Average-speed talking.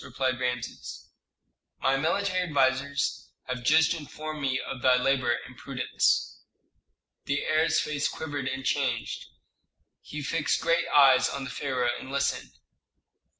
No: slow, 130 wpm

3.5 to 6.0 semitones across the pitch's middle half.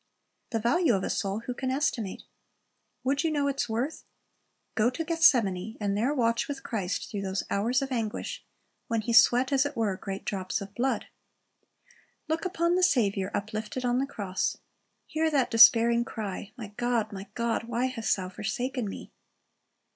Yes: average, 4.3 semitones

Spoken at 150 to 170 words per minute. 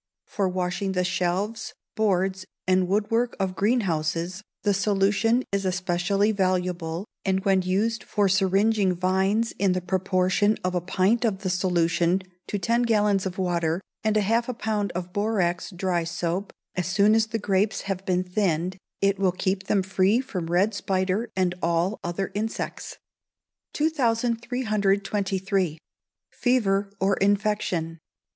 No: average, 140 wpm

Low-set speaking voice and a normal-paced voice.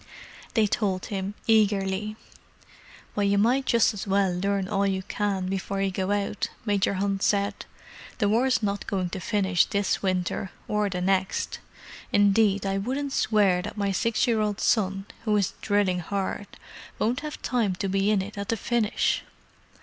No: high, 200 Hz; average, 165 wpm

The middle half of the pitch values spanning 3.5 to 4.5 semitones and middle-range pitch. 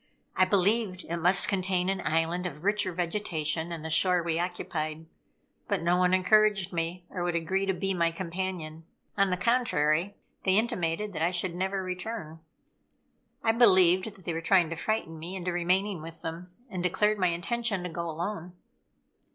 No: narrow, 2.6 semitones; medium, 180 Hz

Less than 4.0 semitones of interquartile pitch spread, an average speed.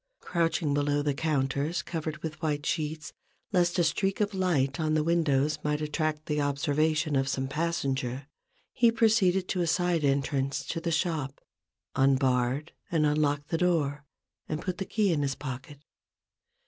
Yes: average, 3.1 semitones; average, 160 wpm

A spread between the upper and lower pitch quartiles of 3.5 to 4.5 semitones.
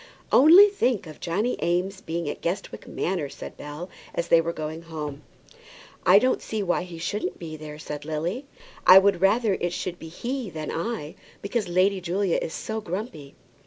Yes: average, 4.0 semitones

